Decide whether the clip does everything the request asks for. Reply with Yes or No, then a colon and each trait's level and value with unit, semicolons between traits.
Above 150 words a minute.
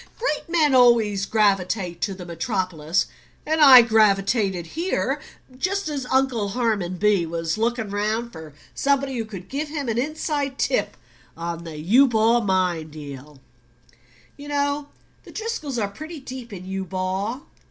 No: average, 140 wpm